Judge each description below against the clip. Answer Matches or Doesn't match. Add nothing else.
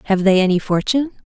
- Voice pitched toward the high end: Matches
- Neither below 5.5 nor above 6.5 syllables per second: Doesn't match